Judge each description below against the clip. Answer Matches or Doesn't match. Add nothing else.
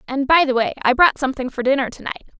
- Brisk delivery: Matches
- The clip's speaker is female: Matches